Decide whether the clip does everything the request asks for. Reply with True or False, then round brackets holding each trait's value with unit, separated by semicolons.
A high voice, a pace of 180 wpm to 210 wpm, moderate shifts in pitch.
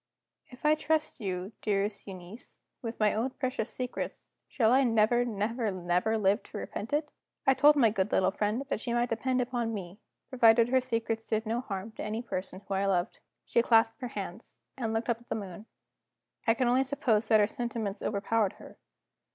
True (225 Hz; 195 wpm; 3.1 semitones)